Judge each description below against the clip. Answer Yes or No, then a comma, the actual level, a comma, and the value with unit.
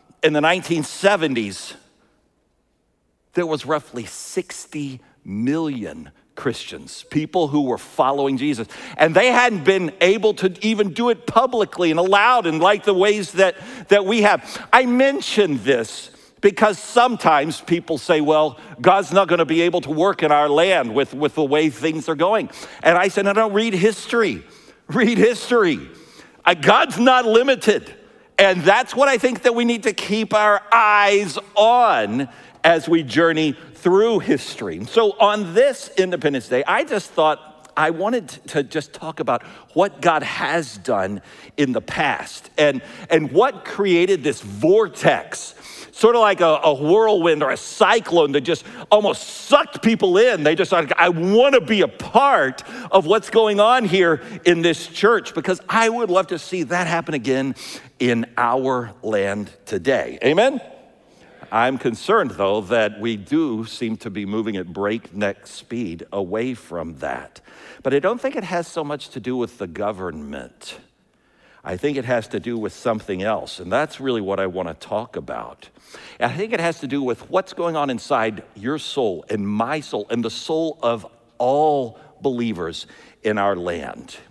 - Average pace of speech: Yes, average, 165 wpm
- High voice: No, medium, 170 Hz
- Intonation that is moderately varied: No, wide, 7.1 semitones